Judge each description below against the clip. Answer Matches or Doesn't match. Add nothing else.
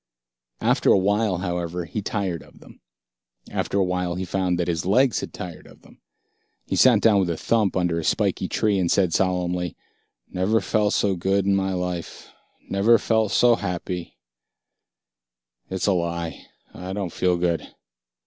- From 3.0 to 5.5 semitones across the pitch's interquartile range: Doesn't match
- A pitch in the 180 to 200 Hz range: Doesn't match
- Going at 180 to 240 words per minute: Doesn't match